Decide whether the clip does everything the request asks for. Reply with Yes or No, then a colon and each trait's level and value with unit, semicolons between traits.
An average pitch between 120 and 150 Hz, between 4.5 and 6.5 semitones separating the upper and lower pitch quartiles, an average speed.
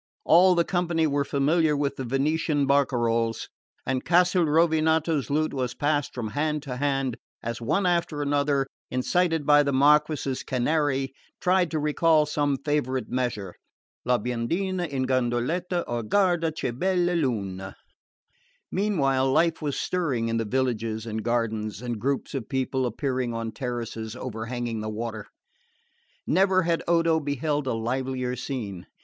Yes: medium, 140 Hz; average, 4.8 semitones; average, 145 wpm